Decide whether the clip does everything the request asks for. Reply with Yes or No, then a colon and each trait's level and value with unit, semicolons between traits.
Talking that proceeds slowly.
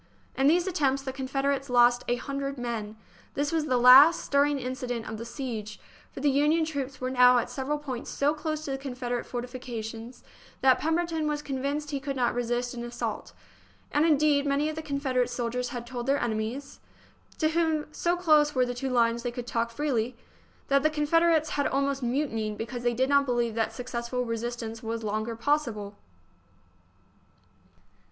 No: average, 180 wpm